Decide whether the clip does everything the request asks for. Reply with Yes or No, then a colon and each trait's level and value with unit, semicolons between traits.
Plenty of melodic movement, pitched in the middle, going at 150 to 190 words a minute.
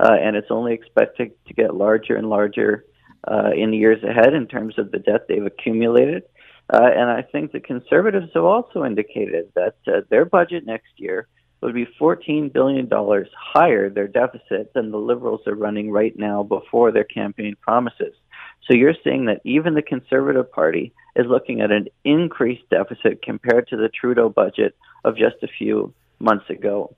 No: wide, 7.9 semitones; low, 125 Hz; average, 185 wpm